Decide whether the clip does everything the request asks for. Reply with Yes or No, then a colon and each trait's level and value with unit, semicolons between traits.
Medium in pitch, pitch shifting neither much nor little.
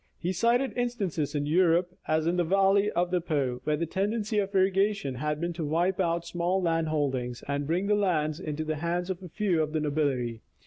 Yes: medium, 170 Hz; average, 4.0 semitones